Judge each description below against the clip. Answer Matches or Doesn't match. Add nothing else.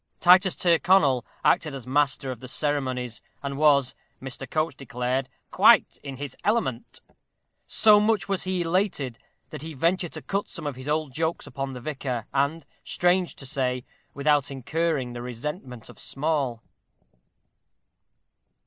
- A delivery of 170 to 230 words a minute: Doesn't match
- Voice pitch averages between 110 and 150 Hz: Matches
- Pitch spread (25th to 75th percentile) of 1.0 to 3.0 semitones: Doesn't match